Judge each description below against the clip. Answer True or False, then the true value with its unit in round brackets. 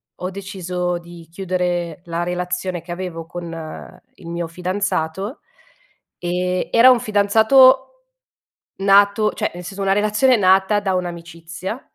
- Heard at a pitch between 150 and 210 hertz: True (185 Hz)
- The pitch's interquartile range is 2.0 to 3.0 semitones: True (2.7 semitones)